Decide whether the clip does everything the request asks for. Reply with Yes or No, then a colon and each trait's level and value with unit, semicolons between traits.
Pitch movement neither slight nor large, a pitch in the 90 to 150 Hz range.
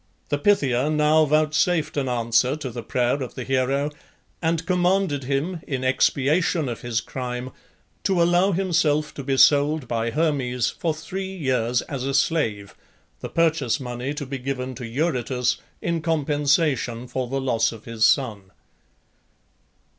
Yes: average, 4.0 semitones; medium, 140 Hz